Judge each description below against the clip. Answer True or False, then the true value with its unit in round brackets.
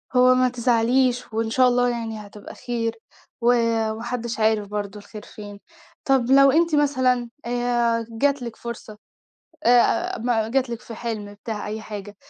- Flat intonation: True (2.3 semitones)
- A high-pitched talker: True (235 Hz)